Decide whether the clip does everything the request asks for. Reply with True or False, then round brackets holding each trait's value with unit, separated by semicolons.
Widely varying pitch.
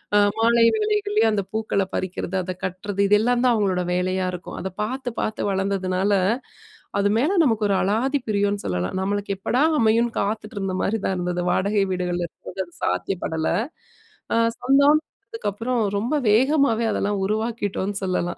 False (3.7 semitones)